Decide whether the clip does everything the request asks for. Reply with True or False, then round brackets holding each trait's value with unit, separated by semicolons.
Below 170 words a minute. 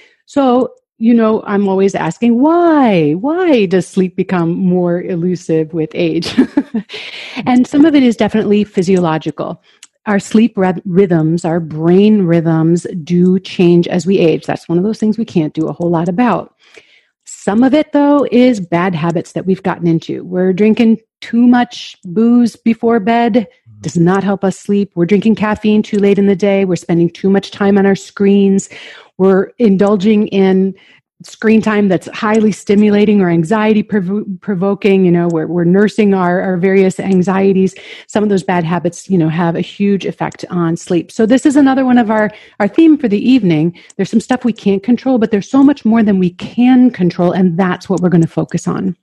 False (190 wpm)